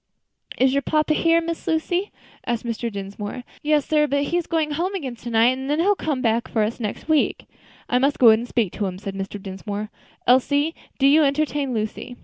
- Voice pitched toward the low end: No, very high, 260 Hz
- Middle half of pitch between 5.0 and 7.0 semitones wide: Yes, wide, 5.5 semitones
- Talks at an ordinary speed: No, fast, 210 wpm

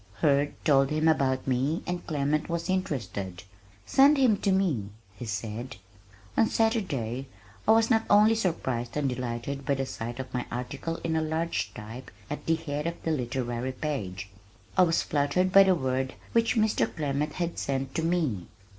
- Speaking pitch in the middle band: Yes, medium, 145 Hz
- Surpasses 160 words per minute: Yes, average, 170 wpm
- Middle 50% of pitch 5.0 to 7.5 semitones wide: Yes, wide, 5.4 semitones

